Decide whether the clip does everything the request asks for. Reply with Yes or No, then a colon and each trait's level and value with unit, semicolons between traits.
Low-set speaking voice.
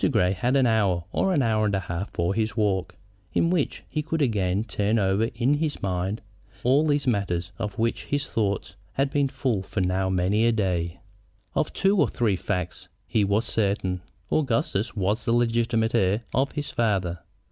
Yes: low, 110 Hz